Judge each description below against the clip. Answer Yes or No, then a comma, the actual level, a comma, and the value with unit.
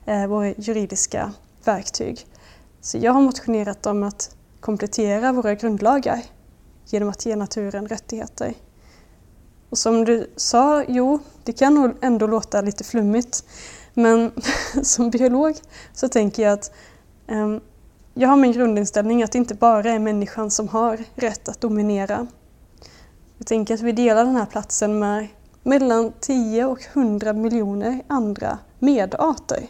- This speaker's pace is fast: No, average, 135 wpm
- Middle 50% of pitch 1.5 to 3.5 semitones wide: Yes, average, 2.9 semitones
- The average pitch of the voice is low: No, high, 230 Hz